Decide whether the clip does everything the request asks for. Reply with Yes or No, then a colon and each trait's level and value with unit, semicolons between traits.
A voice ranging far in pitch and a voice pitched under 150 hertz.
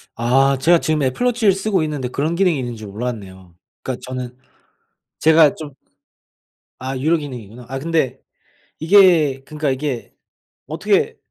No: average, 4.3 semitones; low, 135 Hz